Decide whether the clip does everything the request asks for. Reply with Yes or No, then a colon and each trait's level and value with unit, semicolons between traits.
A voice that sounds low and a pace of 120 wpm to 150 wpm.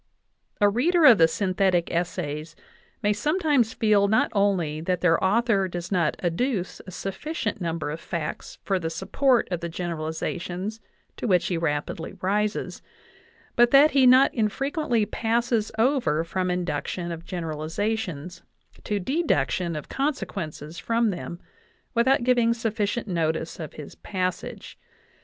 No: high, 190 Hz; slow, 135 wpm